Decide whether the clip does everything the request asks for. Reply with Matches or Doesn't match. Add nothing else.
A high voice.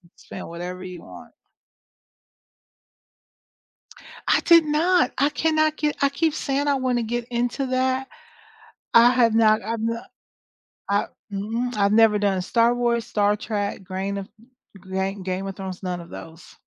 Matches